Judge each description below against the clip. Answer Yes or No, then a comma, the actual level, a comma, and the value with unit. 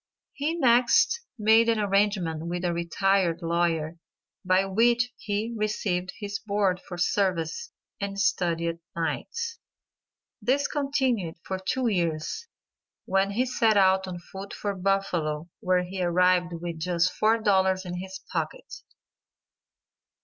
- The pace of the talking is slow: Yes, slow, 125 wpm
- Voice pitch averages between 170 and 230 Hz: Yes, high, 190 Hz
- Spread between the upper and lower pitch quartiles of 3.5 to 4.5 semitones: Yes, average, 3.8 semitones